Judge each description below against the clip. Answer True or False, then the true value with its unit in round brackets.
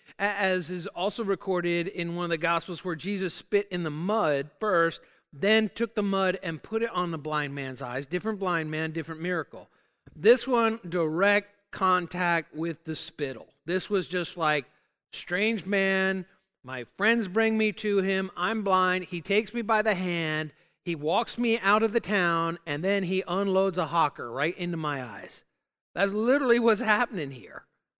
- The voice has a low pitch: False (185 Hz)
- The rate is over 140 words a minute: True (175 wpm)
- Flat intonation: False (3.6 semitones)